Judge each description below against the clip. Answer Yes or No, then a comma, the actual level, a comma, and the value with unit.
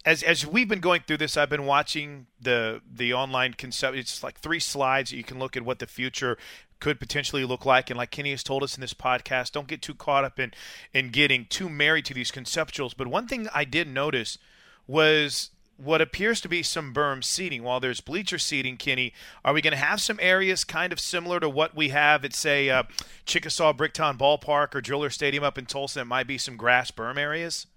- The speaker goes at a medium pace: No, fast, 225 wpm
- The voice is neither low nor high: Yes, medium, 145 Hz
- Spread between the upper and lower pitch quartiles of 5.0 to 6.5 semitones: No, average, 3.5 semitones